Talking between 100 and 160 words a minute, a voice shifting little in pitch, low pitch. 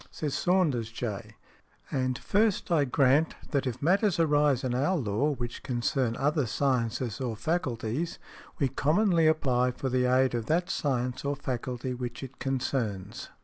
No: average, 155 wpm; average, 3.5 semitones; low, 130 Hz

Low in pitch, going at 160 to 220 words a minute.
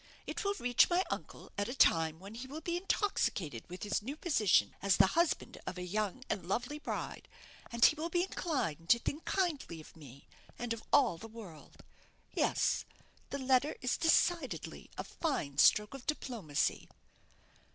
No: high, 240 Hz; average, 170 wpm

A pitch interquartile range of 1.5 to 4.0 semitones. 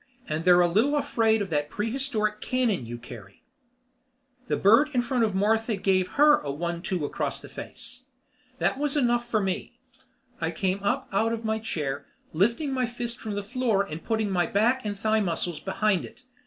No: average, 5.1 semitones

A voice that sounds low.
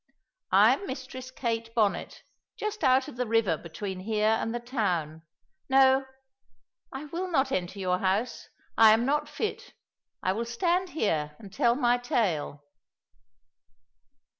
No: high, 235 Hz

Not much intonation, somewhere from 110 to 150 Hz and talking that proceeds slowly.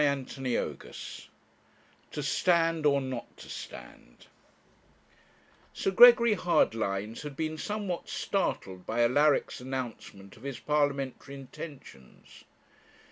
No: average, 5.2 semitones; medium, 140 Hz; slow, 100 wpm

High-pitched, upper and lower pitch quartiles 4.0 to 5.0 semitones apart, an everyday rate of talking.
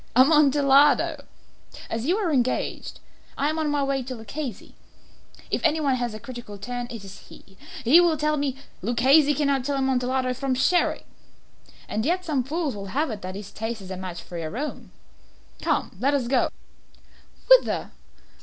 Yes: very high, 265 Hz; average, 4.4 semitones; average, 175 wpm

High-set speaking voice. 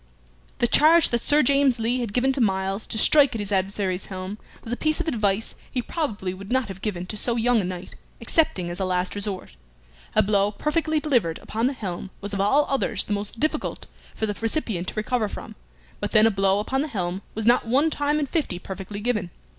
Yes: high, 220 Hz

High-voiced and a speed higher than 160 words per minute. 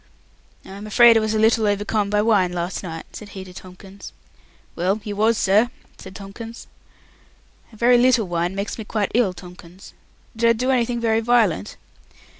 Yes: high, 210 Hz; average, 180 wpm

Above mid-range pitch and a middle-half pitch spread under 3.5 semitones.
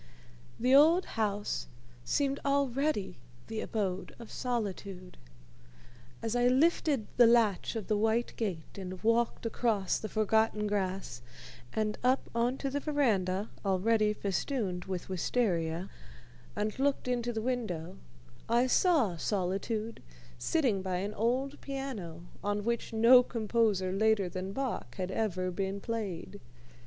No: high, 220 Hz; average, 4.2 semitones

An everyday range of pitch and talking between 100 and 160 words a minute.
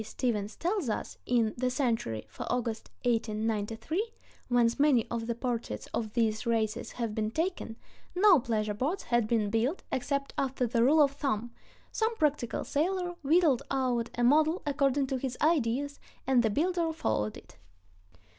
Yes: average, 4.5 semitones; average, 155 wpm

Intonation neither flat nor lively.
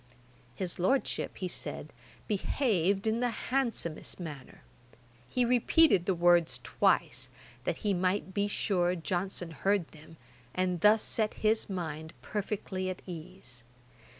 Yes: average, 3.4 semitones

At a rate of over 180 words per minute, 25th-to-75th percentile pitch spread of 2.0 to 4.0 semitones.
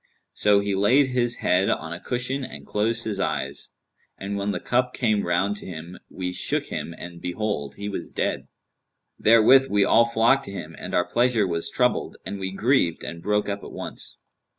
No: average, 195 wpm; average, 4.5 semitones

